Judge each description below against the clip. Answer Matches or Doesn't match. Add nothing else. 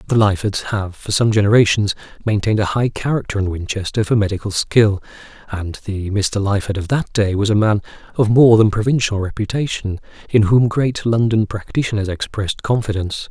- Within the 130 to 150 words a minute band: Doesn't match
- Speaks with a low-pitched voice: Matches